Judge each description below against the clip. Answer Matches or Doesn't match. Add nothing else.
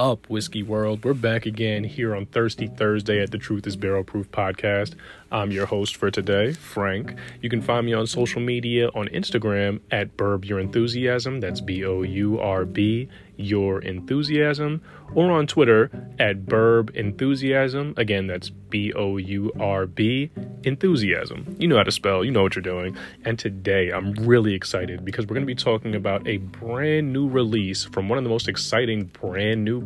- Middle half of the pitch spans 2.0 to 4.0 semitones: Matches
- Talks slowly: Doesn't match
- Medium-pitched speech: Doesn't match